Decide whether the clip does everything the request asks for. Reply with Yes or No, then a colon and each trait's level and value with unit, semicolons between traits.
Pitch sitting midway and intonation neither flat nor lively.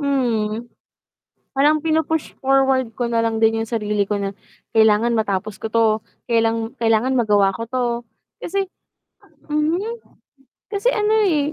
No: high, 235 Hz; average, 4.9 semitones